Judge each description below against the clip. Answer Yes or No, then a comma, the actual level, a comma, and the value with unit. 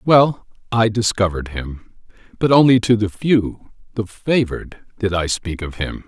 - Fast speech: No, average, 160 wpm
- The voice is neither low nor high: No, low, 105 Hz